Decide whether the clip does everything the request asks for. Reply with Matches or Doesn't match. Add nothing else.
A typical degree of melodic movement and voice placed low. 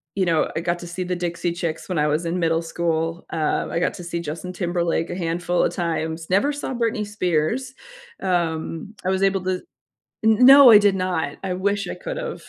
Doesn't match